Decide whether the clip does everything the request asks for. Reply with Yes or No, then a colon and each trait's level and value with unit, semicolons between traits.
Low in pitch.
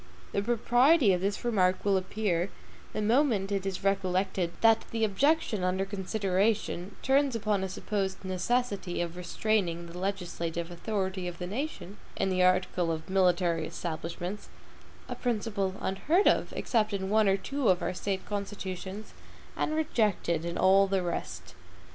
No: high, 195 Hz